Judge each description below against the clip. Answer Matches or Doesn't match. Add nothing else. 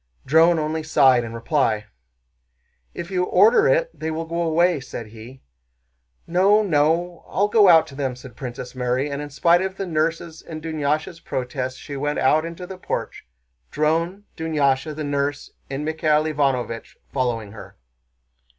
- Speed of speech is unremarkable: Matches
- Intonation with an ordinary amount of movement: Matches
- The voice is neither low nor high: Matches